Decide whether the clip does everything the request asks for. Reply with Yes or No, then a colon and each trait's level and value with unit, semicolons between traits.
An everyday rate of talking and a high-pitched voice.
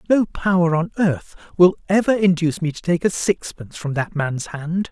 No: average, 195 wpm; medium, 170 Hz